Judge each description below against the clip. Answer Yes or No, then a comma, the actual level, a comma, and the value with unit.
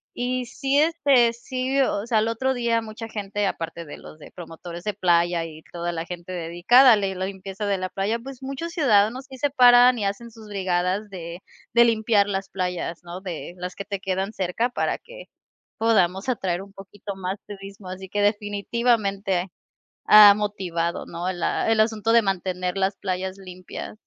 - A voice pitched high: Yes, high, 200 Hz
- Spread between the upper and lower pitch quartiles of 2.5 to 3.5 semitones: No, average, 3.9 semitones